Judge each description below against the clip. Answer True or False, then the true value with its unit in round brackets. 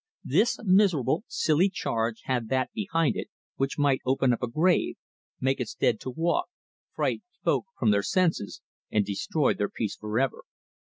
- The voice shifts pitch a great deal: True (6.4 semitones)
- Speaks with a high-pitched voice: False (135 Hz)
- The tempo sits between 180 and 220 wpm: False (165 wpm)